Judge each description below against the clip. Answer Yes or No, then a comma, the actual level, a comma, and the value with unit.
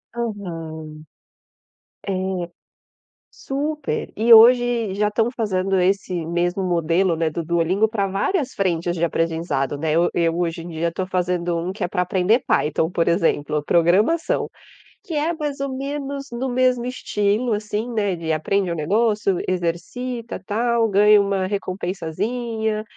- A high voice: Yes, high, 195 Hz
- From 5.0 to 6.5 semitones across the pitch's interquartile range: Yes, wide, 5.4 semitones